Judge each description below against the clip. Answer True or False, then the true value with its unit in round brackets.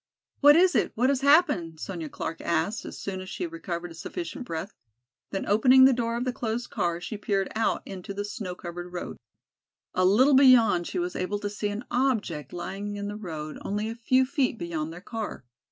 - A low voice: False (205 Hz)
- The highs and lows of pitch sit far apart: True (5.9 semitones)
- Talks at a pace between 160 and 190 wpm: False (205 wpm)